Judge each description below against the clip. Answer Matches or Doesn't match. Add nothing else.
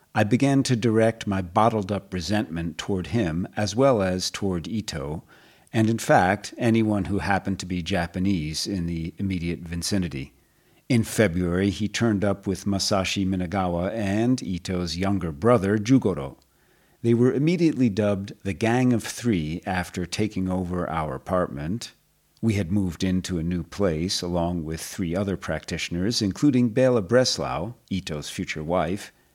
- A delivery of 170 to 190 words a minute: Doesn't match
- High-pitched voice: Doesn't match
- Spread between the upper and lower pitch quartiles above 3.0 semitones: Matches